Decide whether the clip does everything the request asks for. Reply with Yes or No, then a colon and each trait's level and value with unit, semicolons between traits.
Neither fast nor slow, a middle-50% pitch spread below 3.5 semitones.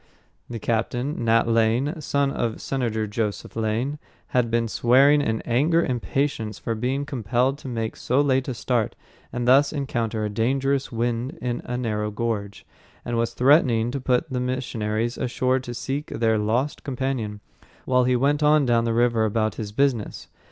Yes: average, 165 wpm; average, 3.1 semitones